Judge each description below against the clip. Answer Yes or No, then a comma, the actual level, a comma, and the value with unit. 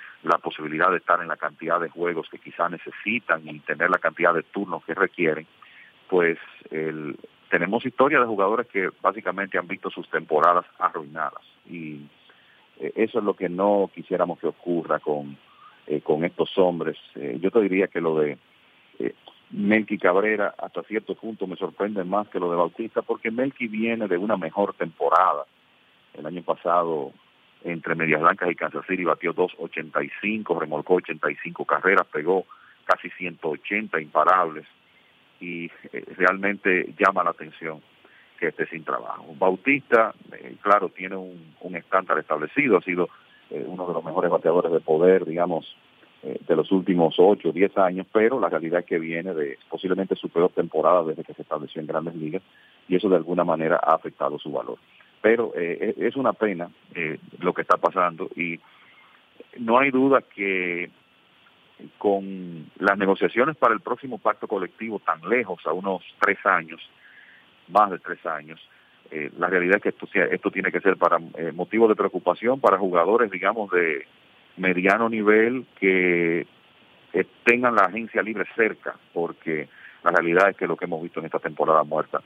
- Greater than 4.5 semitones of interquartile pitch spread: No, average, 3.4 semitones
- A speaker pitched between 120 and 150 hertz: No, very low, 90 Hz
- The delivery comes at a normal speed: Yes, average, 170 wpm